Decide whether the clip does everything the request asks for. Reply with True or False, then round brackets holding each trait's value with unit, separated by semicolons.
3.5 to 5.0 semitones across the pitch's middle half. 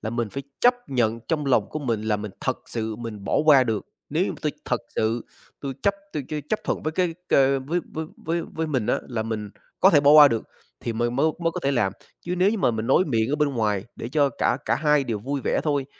False (5.5 semitones)